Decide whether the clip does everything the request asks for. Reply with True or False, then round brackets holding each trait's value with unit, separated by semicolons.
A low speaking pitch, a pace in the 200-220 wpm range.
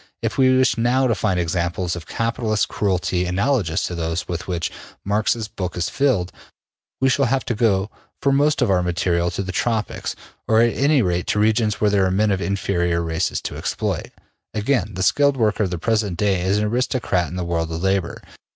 True (100 Hz; 205 wpm)